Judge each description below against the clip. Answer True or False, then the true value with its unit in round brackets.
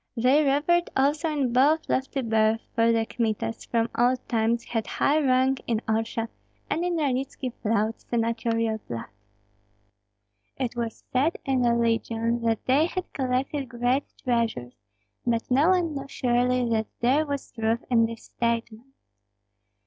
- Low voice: False (245 Hz)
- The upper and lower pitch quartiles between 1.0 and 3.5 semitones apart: True (3.1 semitones)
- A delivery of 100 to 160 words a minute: True (145 wpm)